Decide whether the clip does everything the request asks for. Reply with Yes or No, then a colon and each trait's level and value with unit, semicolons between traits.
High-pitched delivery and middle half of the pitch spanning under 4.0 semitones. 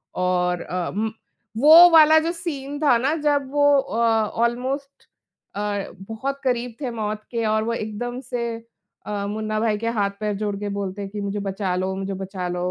No: high, 220 Hz; average, 4.7 semitones